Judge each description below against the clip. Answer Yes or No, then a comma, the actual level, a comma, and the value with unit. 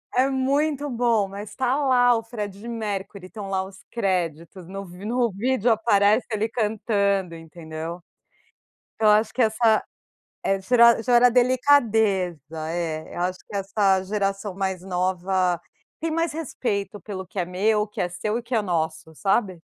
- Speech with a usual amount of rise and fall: Yes, average, 4.2 semitones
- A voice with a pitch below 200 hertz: No, high, 205 Hz